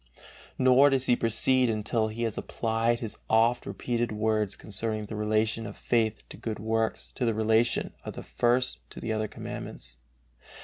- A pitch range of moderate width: No, narrow, 1.6 semitones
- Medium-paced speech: Yes, average, 170 wpm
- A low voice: Yes, low, 110 Hz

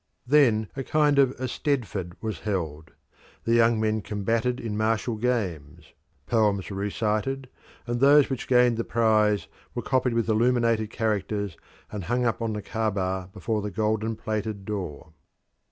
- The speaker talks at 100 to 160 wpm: Yes, average, 150 wpm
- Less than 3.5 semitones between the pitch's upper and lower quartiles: Yes, average, 2.8 semitones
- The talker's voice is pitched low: Yes, low, 110 Hz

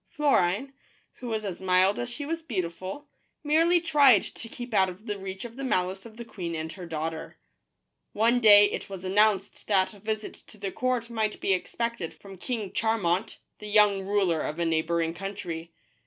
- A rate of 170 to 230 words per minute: Yes, average, 185 wpm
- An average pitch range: Yes, average, 4.1 semitones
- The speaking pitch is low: No, high, 205 Hz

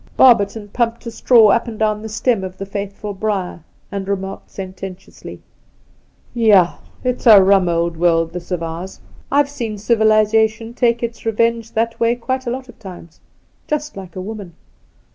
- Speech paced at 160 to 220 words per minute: Yes, average, 175 wpm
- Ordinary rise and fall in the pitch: Yes, average, 3.5 semitones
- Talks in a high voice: Yes, high, 215 Hz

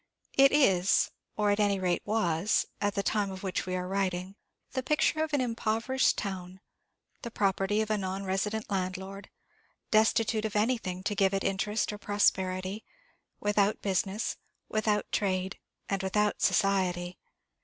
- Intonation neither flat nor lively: No, narrow, 2.3 semitones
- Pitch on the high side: Yes, high, 200 Hz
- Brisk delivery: No, average, 150 wpm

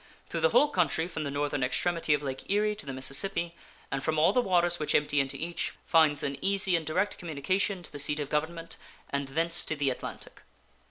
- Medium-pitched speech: Yes, medium, 160 Hz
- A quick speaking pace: Yes, fast, 215 wpm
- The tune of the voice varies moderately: Yes, average, 3.8 semitones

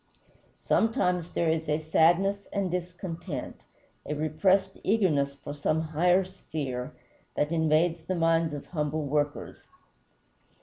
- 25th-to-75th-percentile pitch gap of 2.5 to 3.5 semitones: Yes, average, 3.1 semitones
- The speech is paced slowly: Yes, slow, 120 wpm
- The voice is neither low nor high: Yes, medium, 160 Hz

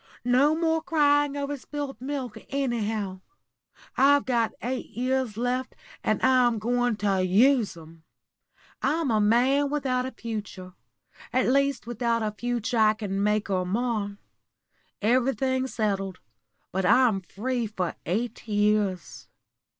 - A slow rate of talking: Yes, slow, 125 wpm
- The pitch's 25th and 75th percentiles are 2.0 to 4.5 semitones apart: Yes, average, 4.0 semitones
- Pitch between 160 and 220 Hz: No, high, 240 Hz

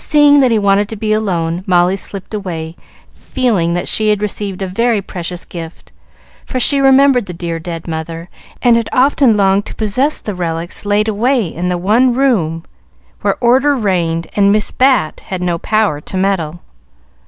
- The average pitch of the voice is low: No, high, 200 Hz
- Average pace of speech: Yes, average, 175 wpm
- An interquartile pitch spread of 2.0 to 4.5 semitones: No, average, 5.2 semitones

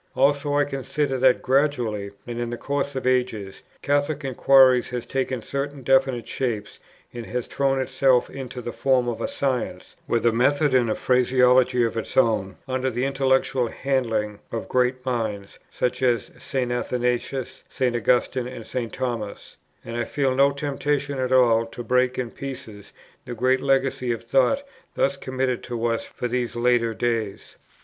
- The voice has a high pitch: No, low, 125 Hz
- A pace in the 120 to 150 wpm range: No, average, 165 wpm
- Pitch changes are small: Yes, narrow, 2.1 semitones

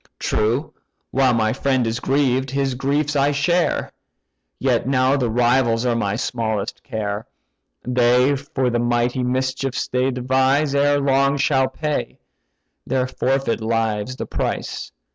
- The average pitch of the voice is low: Yes, low, 130 Hz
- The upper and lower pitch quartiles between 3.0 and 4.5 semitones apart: No, narrow, 2.6 semitones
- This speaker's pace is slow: Yes, slow, 130 wpm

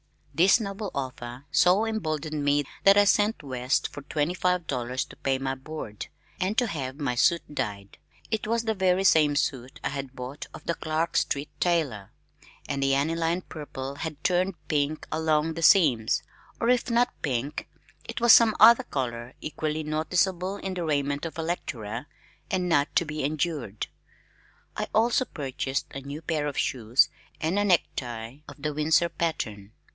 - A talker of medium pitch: Yes, medium, 155 Hz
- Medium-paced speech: Yes, average, 170 wpm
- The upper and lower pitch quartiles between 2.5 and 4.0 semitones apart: No, average, 4.9 semitones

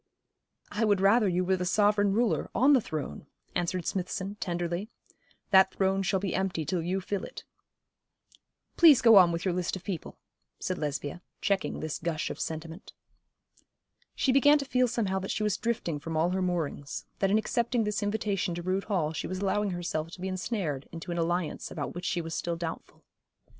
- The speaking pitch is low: No, medium, 185 Hz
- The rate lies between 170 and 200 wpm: Yes, average, 190 wpm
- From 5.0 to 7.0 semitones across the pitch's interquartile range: No, average, 3.2 semitones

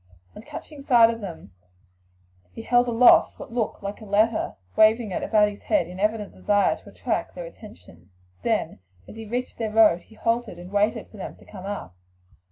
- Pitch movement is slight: Yes, narrow, 2.3 semitones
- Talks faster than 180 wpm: Yes, average, 190 wpm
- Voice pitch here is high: Yes, high, 215 Hz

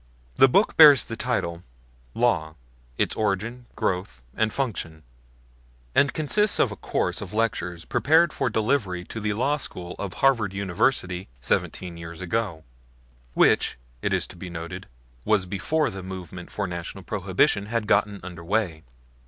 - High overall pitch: No, low, 100 Hz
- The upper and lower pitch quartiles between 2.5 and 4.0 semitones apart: No, average, 5.3 semitones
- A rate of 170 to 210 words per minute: No, average, 150 wpm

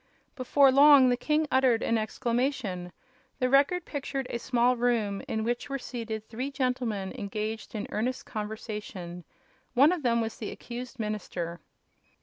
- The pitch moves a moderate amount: Yes, average, 3.4 semitones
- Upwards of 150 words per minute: No, average, 145 wpm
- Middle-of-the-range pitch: No, high, 240 Hz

